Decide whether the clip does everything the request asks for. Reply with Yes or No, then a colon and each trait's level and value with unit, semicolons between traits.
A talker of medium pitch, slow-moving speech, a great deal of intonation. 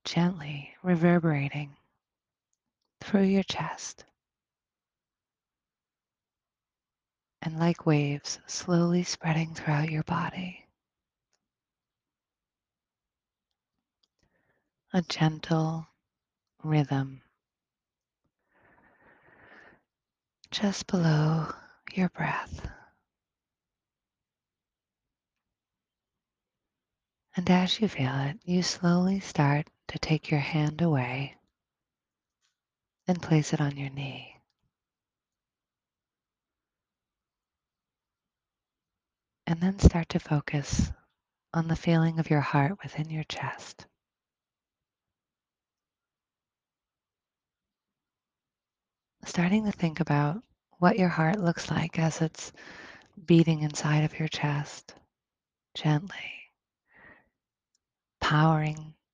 No: medium, 160 Hz; slow, 70 wpm; average, 3.1 semitones